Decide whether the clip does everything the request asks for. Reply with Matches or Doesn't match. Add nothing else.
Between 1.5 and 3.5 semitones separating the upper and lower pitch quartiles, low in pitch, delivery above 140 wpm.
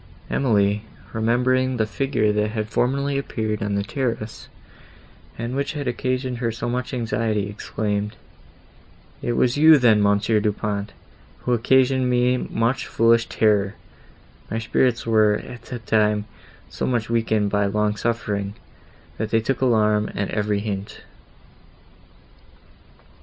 Doesn't match